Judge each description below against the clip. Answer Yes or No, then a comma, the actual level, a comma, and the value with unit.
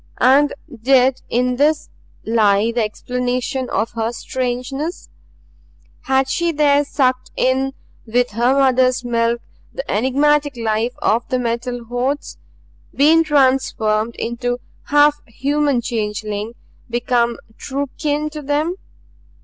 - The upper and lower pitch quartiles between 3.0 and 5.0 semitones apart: Yes, average, 3.3 semitones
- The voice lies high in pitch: Yes, very high, 255 Hz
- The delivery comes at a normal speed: No, slow, 115 wpm